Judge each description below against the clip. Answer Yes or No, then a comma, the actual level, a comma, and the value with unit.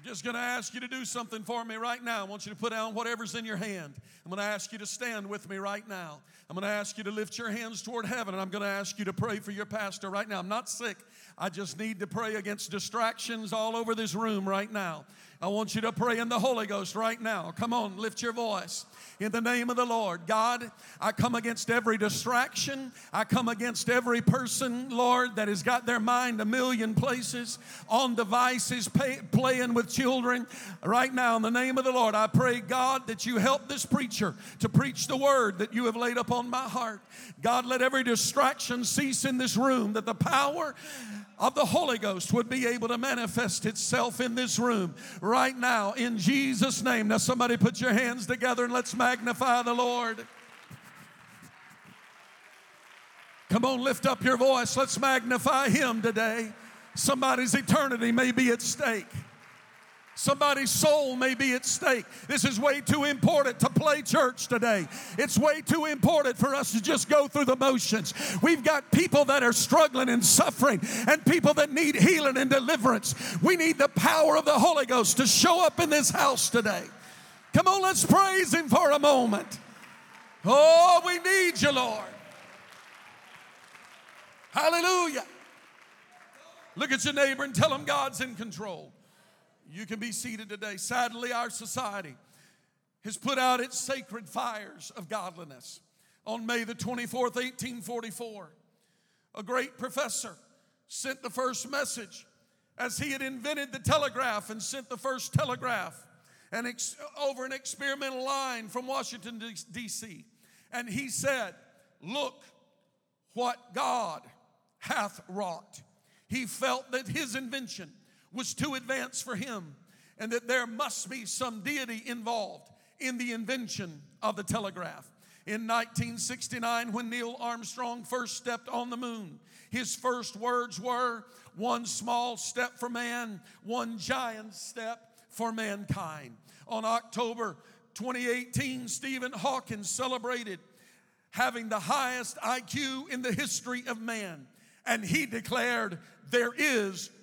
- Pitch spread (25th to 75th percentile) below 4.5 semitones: Yes, average, 3.0 semitones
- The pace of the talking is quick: No, average, 165 wpm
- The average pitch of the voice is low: No, high, 240 Hz